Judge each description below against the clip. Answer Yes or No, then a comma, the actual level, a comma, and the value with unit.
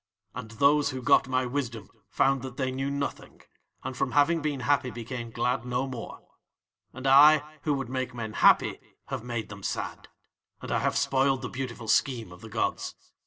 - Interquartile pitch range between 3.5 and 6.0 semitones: No, narrow, 2.6 semitones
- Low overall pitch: Yes, low, 130 Hz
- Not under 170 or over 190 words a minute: Yes, average, 185 wpm